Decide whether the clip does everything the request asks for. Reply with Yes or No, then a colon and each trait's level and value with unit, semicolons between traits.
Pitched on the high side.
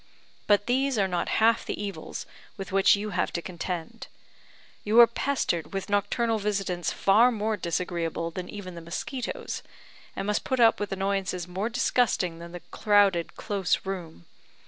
Yes: high, 195 Hz